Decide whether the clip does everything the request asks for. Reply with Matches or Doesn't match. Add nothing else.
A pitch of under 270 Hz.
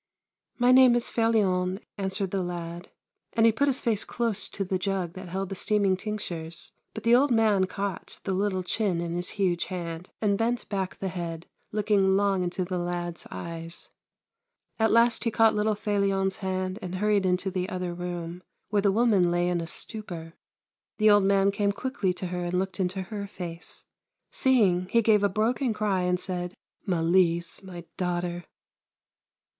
Matches